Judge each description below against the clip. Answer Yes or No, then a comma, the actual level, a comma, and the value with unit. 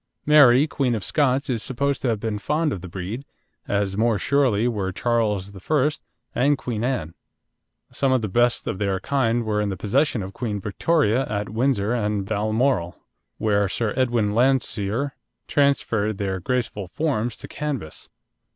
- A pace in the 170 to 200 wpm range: No, average, 160 wpm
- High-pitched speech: No, low, 115 Hz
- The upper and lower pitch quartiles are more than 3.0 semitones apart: Yes, average, 4.5 semitones